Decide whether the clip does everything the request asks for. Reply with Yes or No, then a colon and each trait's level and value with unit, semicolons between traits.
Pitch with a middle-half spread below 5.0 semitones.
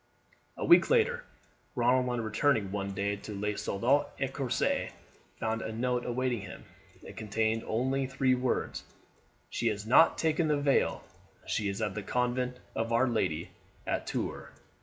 Yes: average, 3.4 semitones